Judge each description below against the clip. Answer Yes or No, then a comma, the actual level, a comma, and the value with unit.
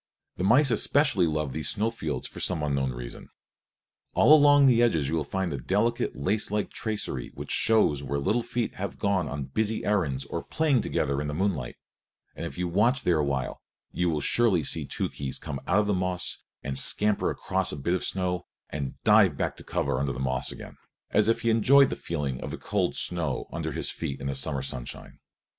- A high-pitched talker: No, very low, 90 Hz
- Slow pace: No, average, 200 wpm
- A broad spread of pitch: Yes, wide, 7.7 semitones